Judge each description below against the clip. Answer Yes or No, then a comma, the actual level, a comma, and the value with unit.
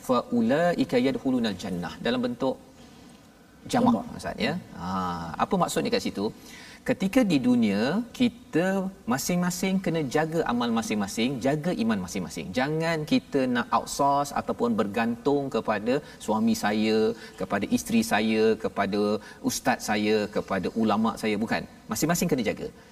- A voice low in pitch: No, high, 195 Hz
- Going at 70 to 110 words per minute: No, average, 120 wpm